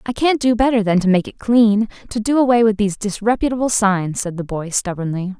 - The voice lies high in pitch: Yes, high, 215 Hz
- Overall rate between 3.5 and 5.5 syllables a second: No, 5.7 syllables/s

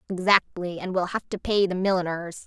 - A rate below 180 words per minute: No, average, 195 wpm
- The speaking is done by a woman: Yes, female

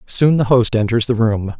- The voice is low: Yes, low, 115 Hz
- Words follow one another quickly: Yes, fast, 225 wpm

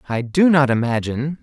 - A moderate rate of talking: Yes, average, 170 wpm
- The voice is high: No, low, 135 Hz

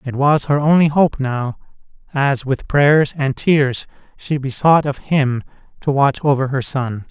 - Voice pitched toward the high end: No, medium, 140 Hz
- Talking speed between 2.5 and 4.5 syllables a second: Yes, 4.0 syllables/s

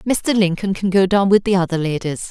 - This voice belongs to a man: No, female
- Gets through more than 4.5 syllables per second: Yes, 5.3 syllables/s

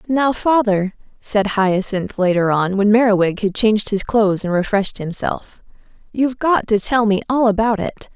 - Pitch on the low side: No, high, 210 Hz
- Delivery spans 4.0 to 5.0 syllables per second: Yes, 4.9 syllables/s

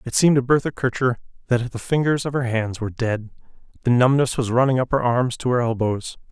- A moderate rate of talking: No, fast, 220 wpm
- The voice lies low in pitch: Yes, low, 125 Hz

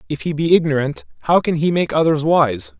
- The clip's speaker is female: No, male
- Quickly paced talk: Yes, fast, 215 wpm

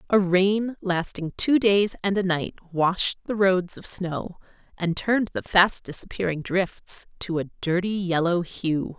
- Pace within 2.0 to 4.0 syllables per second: Yes, 3.9 syllables/s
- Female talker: Yes, female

